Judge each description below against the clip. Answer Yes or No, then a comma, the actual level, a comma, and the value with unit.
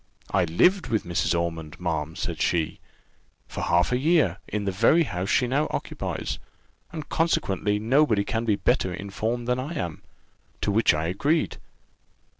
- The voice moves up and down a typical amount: No, wide, 6.9 semitones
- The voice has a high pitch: No, low, 105 Hz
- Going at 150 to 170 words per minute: Yes, average, 160 wpm